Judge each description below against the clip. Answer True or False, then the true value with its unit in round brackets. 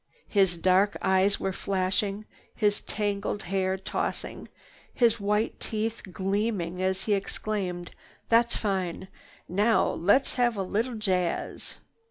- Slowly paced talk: True (120 wpm)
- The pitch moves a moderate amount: False (2.3 semitones)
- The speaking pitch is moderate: False (200 Hz)